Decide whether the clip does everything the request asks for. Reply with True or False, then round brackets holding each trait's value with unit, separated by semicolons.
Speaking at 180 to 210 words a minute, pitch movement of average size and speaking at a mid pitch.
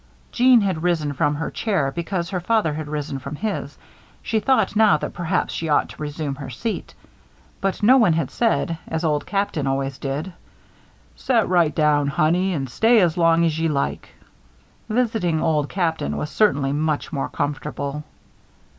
False (170 wpm; 4.9 semitones; 160 Hz)